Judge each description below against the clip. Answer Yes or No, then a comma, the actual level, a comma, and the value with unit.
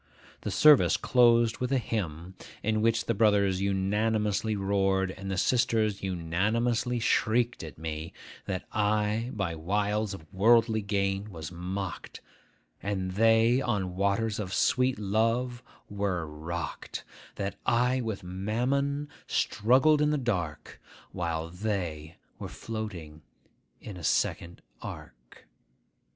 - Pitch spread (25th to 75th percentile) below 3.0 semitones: No, average, 3.7 semitones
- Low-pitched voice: Yes, low, 105 Hz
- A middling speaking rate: No, slow, 120 wpm